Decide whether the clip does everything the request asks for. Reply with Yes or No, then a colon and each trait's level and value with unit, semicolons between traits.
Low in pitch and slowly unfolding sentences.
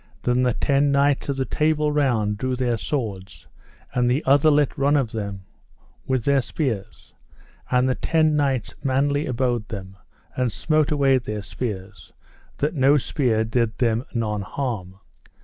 No: low, 130 Hz; average, 155 wpm